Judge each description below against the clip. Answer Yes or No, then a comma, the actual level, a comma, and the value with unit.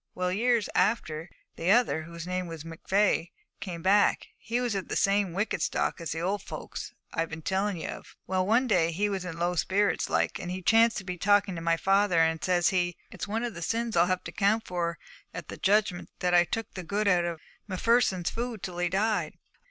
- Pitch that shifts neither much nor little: Yes, average, 3.1 semitones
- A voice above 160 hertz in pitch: Yes, medium, 185 Hz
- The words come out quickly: Yes, fast, 220 wpm